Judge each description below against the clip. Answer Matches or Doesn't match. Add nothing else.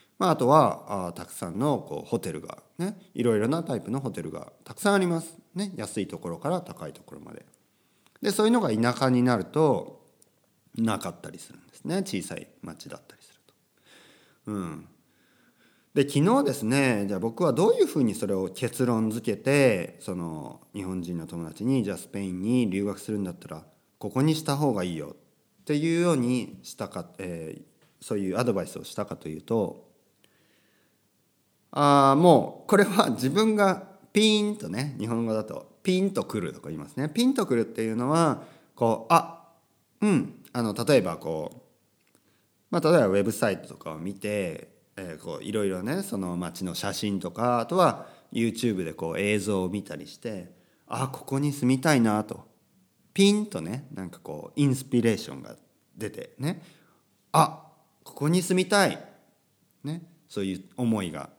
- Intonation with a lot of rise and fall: Matches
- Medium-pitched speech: Doesn't match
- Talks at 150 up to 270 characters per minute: Doesn't match